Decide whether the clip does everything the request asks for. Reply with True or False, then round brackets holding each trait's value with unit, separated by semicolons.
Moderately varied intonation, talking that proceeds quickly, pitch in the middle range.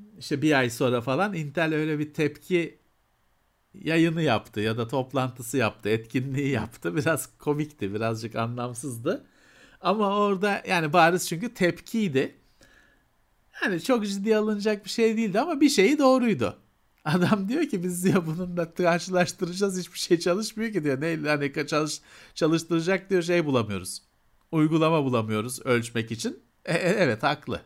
False (6.3 semitones; 145 wpm; 160 Hz)